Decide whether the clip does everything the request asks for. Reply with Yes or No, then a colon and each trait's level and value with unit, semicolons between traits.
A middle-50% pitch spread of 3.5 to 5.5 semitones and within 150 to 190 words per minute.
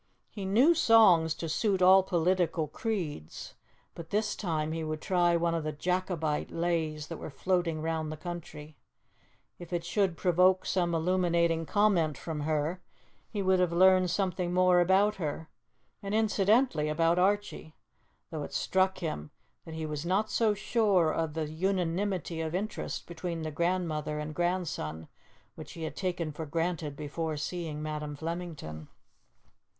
No: average, 3.0 semitones; average, 155 wpm